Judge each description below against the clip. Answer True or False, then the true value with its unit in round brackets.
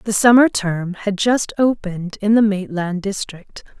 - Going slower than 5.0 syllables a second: True (4.2 syllables/s)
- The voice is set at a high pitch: True (200 Hz)